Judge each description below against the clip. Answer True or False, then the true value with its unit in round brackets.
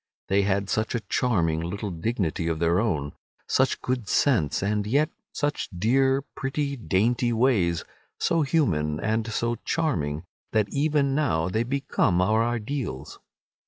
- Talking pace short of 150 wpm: True (140 wpm)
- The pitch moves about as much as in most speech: False (7.1 semitones)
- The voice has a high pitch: False (110 Hz)